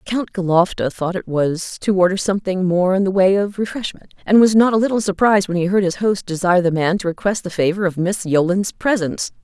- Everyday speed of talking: No, fast, 230 wpm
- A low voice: No, high, 190 Hz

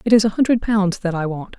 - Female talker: Yes, female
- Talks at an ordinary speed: No, fast, 300 wpm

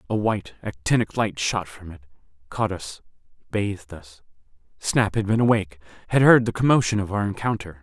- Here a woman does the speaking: No, male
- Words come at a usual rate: Yes, average, 160 wpm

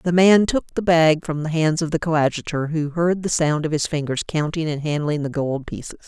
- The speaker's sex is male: No, female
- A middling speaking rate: No, fast, 235 wpm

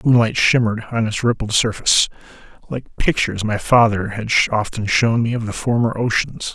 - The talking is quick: No, average, 175 wpm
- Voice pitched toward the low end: Yes, low, 115 Hz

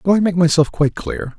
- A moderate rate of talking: No, fast, 260 wpm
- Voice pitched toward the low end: No, medium, 170 Hz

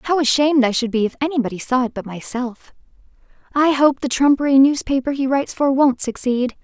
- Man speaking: No, female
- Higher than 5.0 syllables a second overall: Yes, 5.9 syllables/s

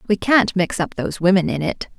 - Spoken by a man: No, female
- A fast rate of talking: Yes, fast, 240 wpm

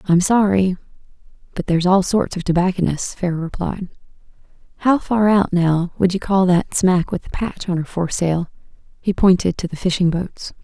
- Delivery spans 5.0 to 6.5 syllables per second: Yes, 5.2 syllables/s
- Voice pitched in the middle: Yes, medium, 180 Hz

